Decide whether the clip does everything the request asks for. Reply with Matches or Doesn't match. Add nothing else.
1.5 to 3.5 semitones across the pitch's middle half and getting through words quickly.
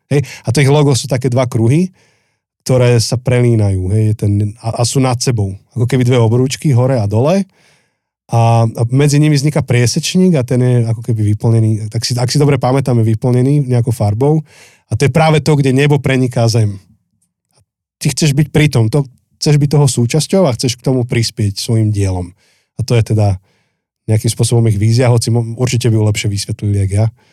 Doesn't match